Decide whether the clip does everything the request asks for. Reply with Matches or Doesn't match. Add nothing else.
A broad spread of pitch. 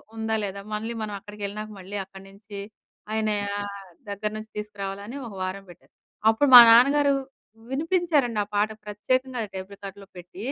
Doesn't match